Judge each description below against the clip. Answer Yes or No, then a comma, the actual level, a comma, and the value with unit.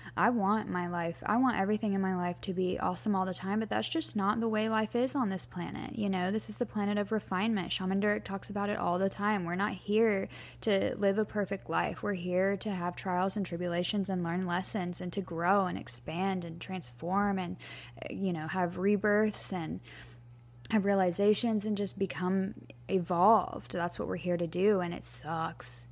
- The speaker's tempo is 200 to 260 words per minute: Yes, fast, 205 wpm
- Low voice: No, high, 195 Hz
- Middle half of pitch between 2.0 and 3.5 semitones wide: Yes, average, 2.8 semitones